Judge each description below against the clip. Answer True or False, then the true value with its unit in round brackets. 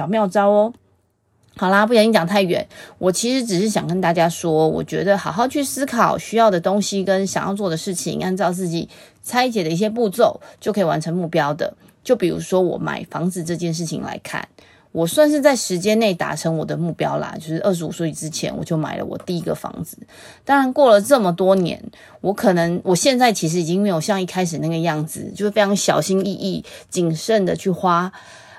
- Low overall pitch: False (190 Hz)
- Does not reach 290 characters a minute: False (315 characters per minute)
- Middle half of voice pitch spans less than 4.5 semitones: True (4.0 semitones)